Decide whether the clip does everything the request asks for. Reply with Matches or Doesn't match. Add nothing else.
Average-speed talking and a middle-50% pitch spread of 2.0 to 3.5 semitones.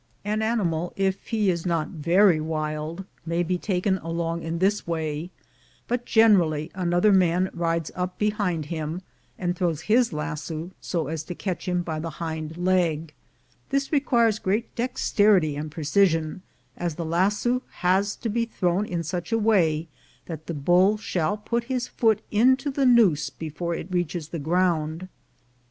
Doesn't match